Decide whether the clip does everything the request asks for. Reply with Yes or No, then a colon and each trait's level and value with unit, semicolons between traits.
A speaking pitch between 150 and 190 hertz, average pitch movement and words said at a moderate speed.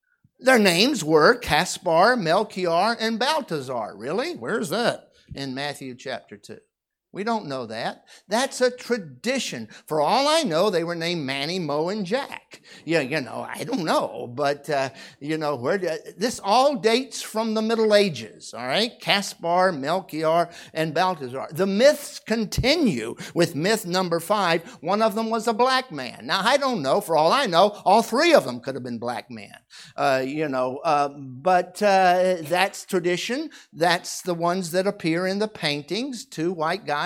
No: medium, 185 Hz; wide, 6.4 semitones; average, 175 wpm